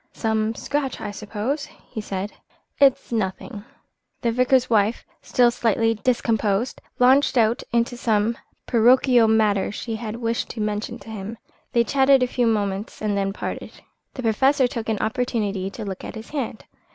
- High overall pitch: Yes, high, 225 Hz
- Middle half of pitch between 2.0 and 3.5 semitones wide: Yes, average, 2.8 semitones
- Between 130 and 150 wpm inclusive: No, average, 160 wpm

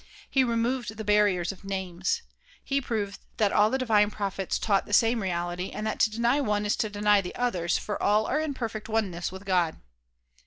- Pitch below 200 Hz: No, high, 210 Hz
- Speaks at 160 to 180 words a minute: No, average, 200 wpm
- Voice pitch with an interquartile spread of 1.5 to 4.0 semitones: Yes, average, 3.1 semitones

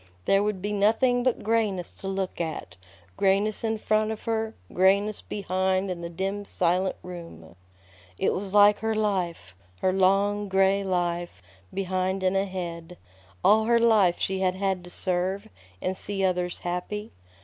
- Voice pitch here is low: No, high, 190 Hz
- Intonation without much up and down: Yes, narrow, 2.3 semitones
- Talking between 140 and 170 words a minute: Yes, average, 155 wpm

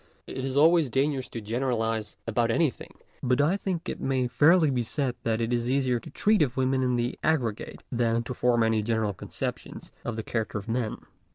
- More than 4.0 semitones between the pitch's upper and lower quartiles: No, average, 3.0 semitones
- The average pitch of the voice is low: Yes, low, 125 Hz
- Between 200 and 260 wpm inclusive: Yes, fast, 205 wpm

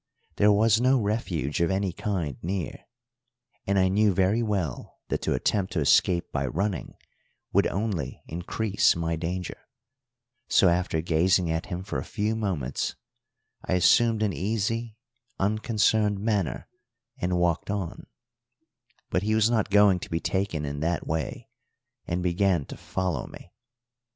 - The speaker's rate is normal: Yes, average, 145 wpm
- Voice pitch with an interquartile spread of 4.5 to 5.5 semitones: No, average, 3.6 semitones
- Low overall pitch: Yes, very low, 95 Hz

